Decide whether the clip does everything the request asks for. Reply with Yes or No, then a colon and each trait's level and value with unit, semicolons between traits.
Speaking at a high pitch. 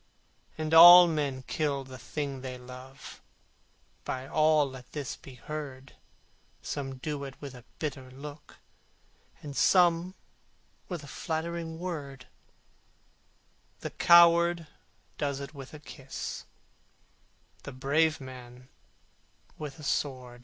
No: medium, 145 Hz